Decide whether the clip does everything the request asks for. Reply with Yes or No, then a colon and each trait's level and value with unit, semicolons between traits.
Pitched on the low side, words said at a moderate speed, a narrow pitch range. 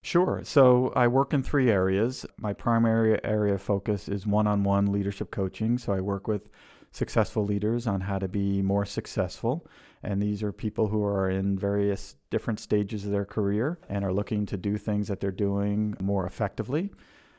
Yes: low, 105 Hz; average, 185 wpm; narrow, 1.9 semitones